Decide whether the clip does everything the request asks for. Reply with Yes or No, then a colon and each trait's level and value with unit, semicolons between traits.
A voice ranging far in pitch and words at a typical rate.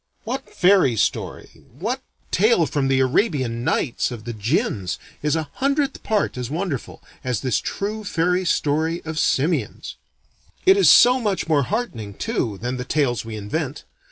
Yes: wide, 8.6 semitones; average, 155 wpm